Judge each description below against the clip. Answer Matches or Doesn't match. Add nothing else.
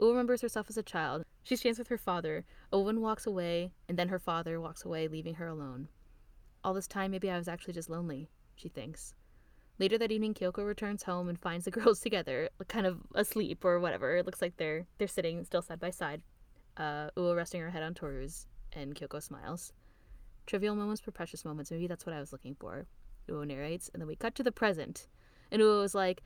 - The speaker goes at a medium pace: Doesn't match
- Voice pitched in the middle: Matches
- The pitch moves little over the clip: Doesn't match